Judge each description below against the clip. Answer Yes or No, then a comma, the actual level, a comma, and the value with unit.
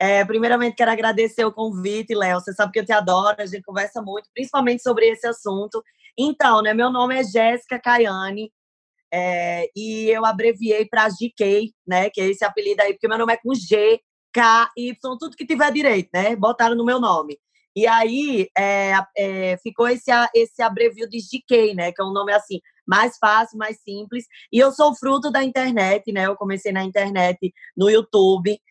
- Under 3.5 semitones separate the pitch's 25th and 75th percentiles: Yes, average, 3.1 semitones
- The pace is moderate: No, fast, 190 wpm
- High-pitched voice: Yes, high, 220 Hz